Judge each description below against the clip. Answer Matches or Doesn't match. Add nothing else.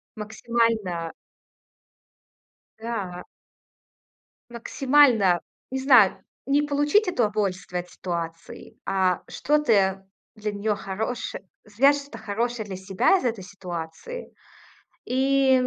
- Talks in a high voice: Matches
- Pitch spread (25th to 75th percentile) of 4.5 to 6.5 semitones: Matches